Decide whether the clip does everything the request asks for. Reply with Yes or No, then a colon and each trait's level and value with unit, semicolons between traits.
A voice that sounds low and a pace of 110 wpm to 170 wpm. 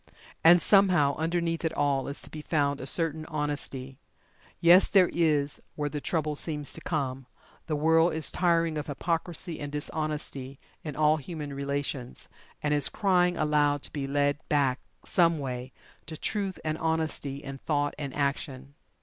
No: medium, 150 Hz; average, 160 wpm